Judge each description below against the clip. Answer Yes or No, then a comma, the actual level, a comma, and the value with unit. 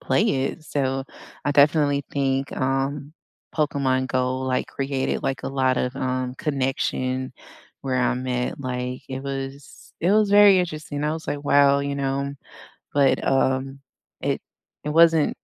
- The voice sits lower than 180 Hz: Yes, low, 135 Hz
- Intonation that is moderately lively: No, narrow, 1.8 semitones